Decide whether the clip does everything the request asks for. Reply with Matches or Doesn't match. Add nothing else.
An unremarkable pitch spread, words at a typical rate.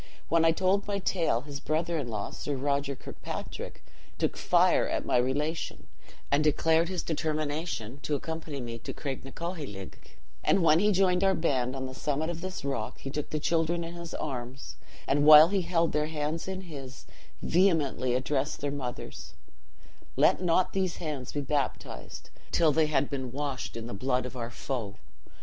Matches